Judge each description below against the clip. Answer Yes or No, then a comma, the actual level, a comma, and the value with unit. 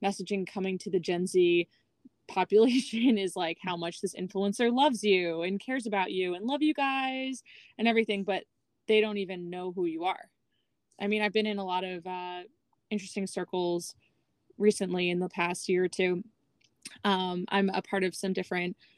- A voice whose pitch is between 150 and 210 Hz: Yes, high, 190 Hz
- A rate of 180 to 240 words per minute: Yes, average, 185 wpm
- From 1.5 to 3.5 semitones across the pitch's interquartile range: Yes, average, 2.8 semitones